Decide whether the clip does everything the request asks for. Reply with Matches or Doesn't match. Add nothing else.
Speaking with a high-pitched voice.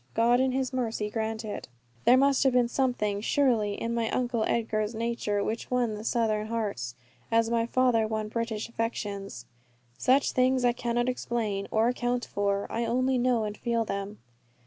Matches